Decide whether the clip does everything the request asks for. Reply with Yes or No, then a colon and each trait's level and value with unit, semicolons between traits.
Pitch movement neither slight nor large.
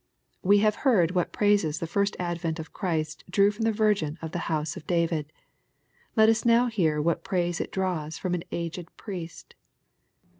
Yes: average, 4.0 semitones